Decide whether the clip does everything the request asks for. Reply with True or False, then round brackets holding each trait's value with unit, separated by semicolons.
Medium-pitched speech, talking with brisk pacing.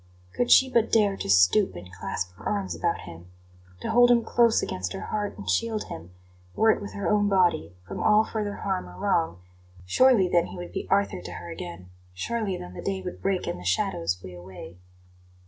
True (175 Hz; 210 wpm)